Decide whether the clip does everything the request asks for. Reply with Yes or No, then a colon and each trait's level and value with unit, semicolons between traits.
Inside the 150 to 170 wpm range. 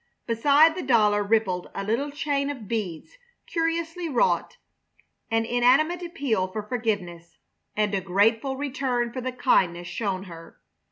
No: slow, 135 wpm